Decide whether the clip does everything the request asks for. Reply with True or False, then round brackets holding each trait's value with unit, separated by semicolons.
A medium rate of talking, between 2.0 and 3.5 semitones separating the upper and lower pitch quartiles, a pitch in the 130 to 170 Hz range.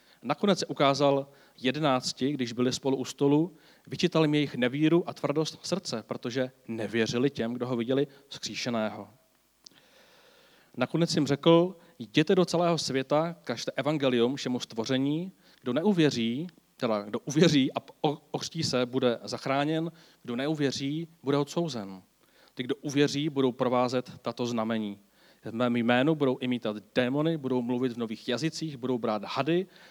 False (140 wpm; 4.1 semitones; 135 Hz)